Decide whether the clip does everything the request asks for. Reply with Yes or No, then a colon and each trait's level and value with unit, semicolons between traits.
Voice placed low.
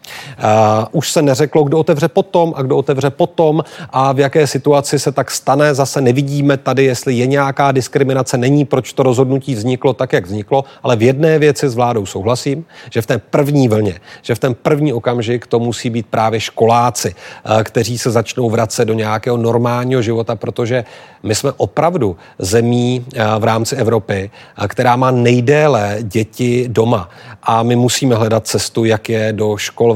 Yes: low, 125 Hz